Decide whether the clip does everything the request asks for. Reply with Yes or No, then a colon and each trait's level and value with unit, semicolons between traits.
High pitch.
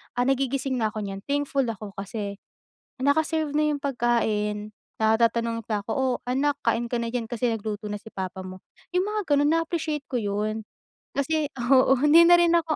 Yes: high, 245 Hz